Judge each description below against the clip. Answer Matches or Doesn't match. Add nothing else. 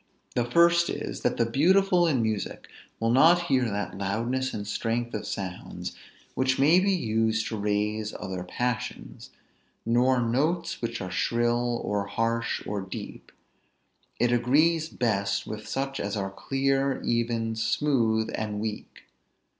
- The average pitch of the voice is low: Matches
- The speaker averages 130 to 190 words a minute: Matches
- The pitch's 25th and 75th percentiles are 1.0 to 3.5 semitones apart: Doesn't match